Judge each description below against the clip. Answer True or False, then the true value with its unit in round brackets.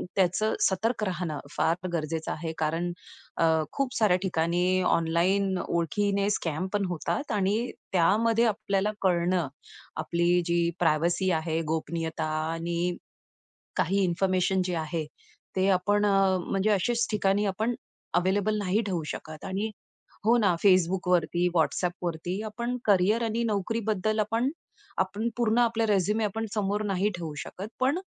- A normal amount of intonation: True (3.5 semitones)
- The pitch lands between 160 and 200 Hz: True (190 Hz)